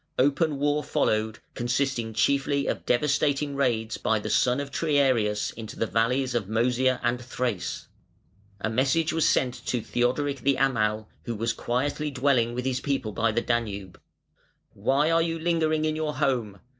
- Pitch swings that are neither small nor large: Yes, average, 3.7 semitones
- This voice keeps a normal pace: Yes, average, 160 wpm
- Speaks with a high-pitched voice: No, low, 130 Hz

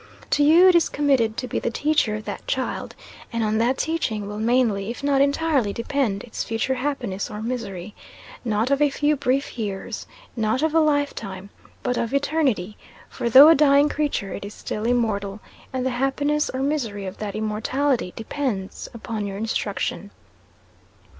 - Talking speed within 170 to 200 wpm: Yes, average, 175 wpm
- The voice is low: No, high, 245 Hz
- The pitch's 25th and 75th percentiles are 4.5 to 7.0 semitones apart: Yes, average, 5.2 semitones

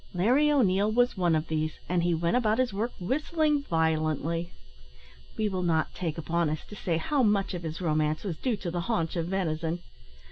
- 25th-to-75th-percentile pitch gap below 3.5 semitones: No, average, 4.8 semitones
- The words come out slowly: No, average, 200 wpm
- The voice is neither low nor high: Yes, medium, 175 Hz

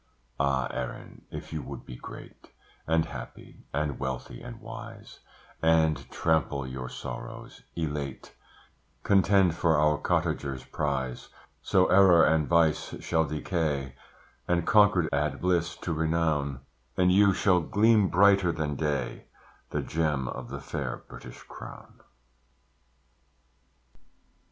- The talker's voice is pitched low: Yes, very low, 80 Hz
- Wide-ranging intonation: No, average, 4.0 semitones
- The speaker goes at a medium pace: No, slow, 120 wpm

